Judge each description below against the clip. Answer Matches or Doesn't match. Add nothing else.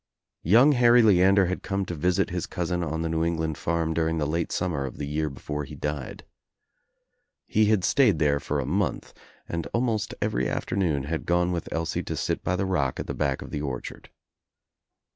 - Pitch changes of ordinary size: Matches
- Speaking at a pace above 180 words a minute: Matches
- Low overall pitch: Matches